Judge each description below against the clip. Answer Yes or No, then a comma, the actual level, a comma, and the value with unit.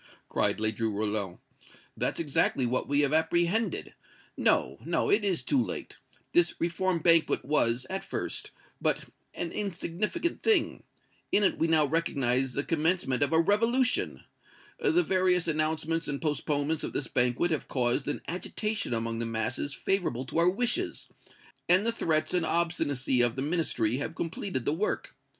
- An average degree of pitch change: No, wide, 5.9 semitones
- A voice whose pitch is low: No, medium, 160 Hz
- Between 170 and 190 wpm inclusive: No, average, 155 wpm